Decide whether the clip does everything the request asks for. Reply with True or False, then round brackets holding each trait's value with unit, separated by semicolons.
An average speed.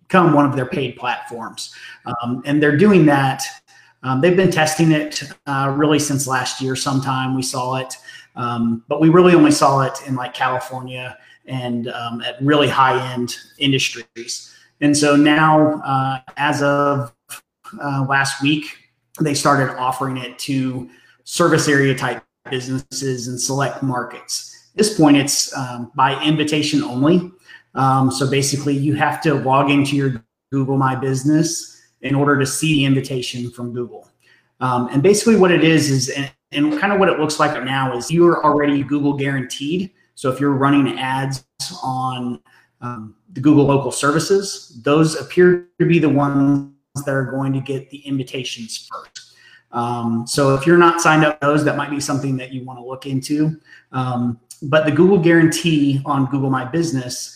True (175 wpm)